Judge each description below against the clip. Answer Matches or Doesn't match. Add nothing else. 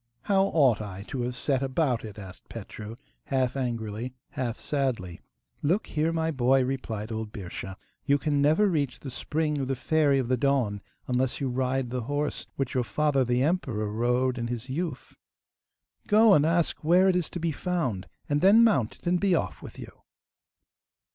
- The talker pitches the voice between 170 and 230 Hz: Doesn't match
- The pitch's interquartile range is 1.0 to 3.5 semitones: Doesn't match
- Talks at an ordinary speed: Matches